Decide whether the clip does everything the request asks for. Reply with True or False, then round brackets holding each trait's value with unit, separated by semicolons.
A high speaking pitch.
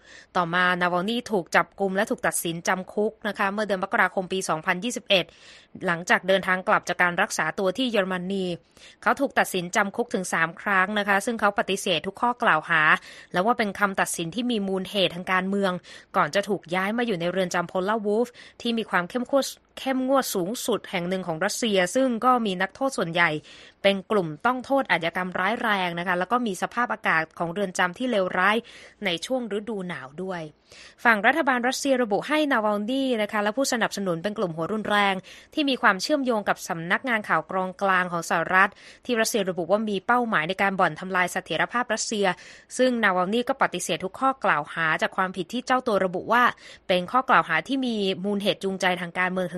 True (195 Hz)